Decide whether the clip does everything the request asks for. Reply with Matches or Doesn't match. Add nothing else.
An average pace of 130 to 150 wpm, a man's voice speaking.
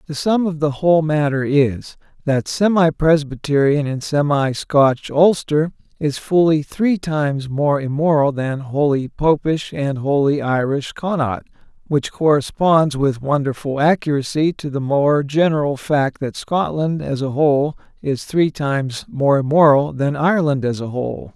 Matches